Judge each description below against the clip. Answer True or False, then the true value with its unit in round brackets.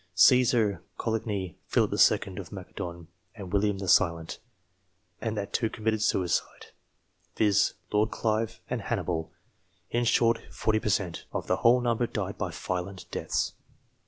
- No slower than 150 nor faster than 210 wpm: False (140 wpm)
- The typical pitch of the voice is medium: False (105 Hz)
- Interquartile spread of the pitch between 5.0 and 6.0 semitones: False (3.4 semitones)